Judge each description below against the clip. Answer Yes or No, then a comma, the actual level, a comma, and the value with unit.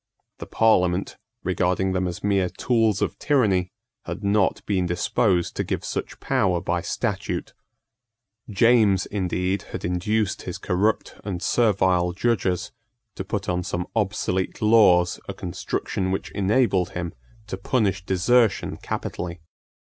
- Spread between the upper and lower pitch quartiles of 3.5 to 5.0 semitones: No, average, 3.0 semitones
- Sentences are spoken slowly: Yes, slow, 130 wpm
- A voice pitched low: Yes, very low, 95 Hz